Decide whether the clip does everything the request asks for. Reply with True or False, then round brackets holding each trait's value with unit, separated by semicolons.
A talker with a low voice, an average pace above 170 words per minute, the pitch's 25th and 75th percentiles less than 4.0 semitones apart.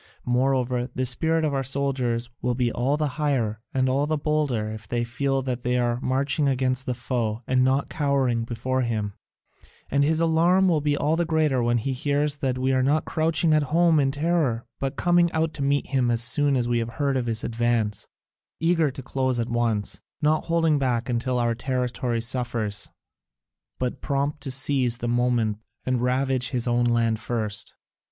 True (130 Hz; 190 wpm; 3.3 semitones)